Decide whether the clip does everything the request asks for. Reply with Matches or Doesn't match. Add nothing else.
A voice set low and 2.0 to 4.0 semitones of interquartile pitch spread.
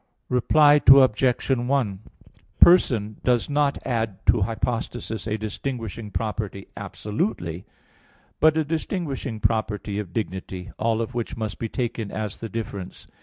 Matches